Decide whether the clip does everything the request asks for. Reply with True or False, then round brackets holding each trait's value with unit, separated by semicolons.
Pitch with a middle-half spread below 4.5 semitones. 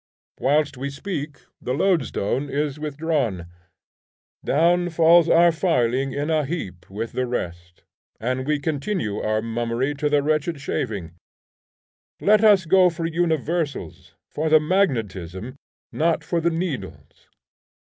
False (5.1 semitones)